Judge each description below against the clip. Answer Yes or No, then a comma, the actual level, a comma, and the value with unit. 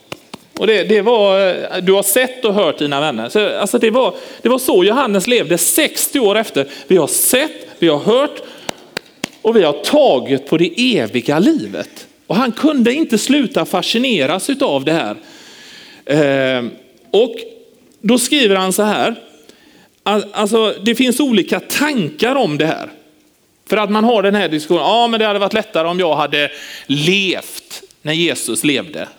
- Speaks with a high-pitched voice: Yes, high, 210 Hz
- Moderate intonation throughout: No, wide, 6.6 semitones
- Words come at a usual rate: Yes, average, 170 wpm